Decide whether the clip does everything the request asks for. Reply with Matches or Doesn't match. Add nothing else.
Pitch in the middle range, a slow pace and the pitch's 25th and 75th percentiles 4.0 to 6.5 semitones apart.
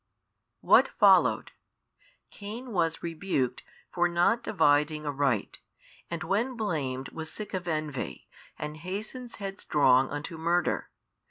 Matches